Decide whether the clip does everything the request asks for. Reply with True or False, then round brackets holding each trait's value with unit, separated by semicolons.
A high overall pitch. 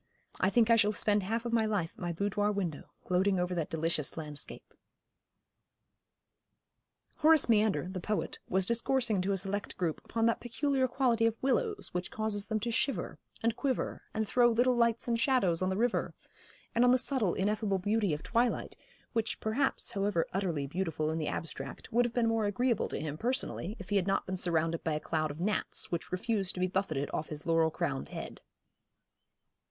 True (205 Hz)